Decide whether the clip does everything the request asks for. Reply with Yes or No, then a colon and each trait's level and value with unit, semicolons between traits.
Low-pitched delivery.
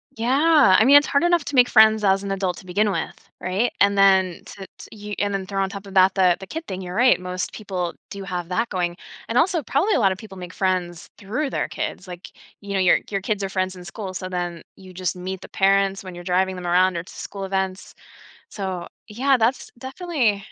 No: high, 195 Hz